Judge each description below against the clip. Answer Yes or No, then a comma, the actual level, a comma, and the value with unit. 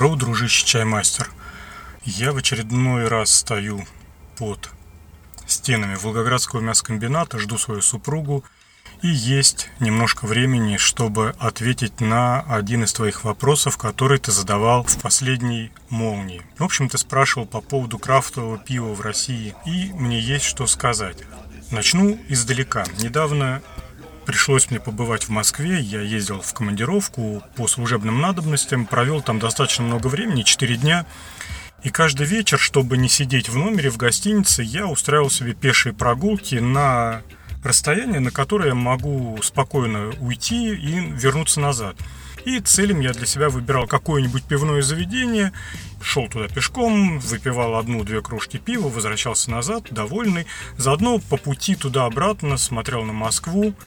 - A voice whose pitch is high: No, low, 125 Hz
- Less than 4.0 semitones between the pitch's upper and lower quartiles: No, average, 4.4 semitones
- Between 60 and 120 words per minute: No, average, 135 wpm